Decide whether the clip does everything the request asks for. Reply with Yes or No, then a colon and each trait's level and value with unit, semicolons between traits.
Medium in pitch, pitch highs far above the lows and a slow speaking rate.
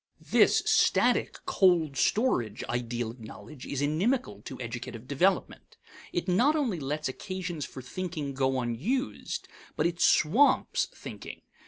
Yes: medium, 150 Hz; wide, 6.8 semitones; slow, 130 wpm